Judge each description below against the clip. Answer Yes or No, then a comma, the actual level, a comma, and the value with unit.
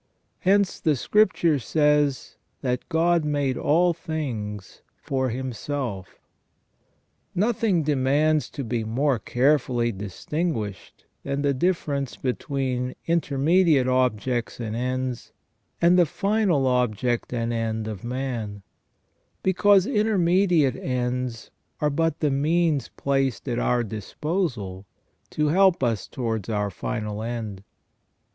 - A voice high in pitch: No, low, 135 Hz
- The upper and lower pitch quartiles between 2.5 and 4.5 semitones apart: No, average, 5.3 semitones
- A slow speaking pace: Yes, slow, 110 wpm